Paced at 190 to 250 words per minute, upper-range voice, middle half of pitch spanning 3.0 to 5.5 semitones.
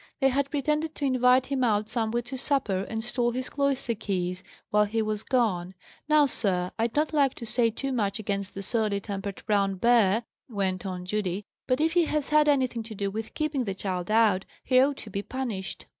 Yes: fast, 205 wpm; high, 225 Hz; average, 4.9 semitones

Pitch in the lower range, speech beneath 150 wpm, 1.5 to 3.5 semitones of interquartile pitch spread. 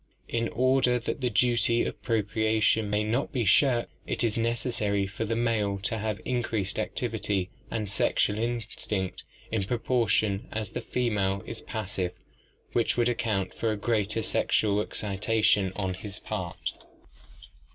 Yes: low, 110 Hz; average, 140 wpm; narrow, 2.5 semitones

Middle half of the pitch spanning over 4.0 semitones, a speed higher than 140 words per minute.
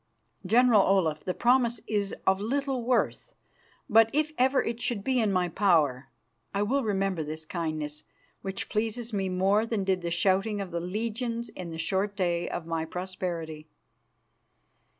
Yes: average, 4.8 semitones; average, 160 wpm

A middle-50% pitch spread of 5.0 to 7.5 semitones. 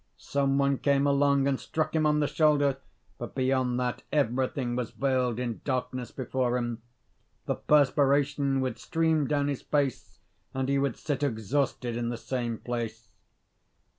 No: narrow, 2.4 semitones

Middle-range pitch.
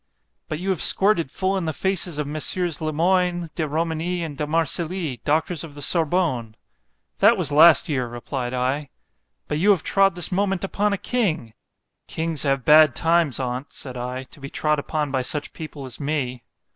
Yes: medium, 155 Hz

